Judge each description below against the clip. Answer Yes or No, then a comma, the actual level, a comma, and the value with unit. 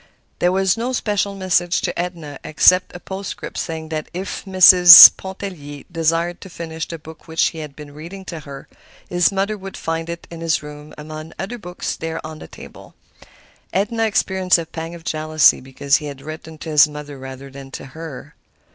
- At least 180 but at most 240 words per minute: Yes, average, 190 wpm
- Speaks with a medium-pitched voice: Yes, medium, 165 Hz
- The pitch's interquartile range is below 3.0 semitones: No, average, 3.3 semitones